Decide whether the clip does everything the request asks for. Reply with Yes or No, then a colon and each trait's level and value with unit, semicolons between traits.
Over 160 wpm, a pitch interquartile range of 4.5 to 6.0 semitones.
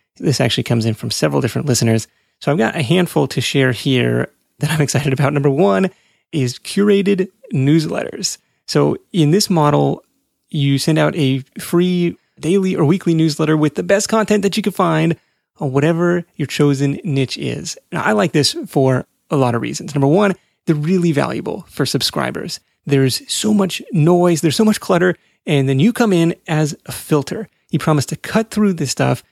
Yes: average, 185 wpm; average, 5.2 semitones